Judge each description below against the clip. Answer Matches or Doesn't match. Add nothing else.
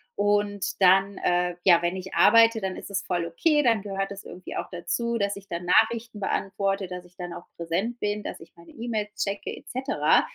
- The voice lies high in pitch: Matches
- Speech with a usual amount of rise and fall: Matches